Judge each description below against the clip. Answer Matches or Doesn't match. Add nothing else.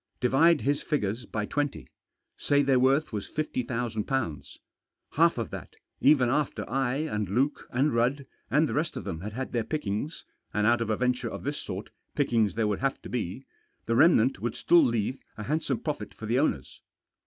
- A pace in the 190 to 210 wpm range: Matches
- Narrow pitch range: Doesn't match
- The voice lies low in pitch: Matches